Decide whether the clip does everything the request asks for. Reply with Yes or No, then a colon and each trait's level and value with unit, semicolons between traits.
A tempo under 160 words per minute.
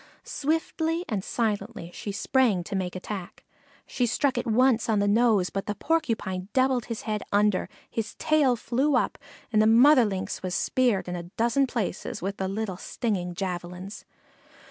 No: average, 165 wpm